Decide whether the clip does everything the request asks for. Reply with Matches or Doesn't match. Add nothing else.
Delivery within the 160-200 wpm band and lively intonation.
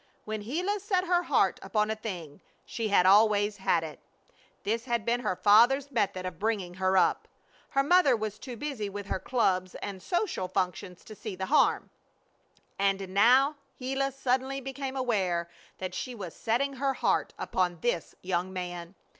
Matches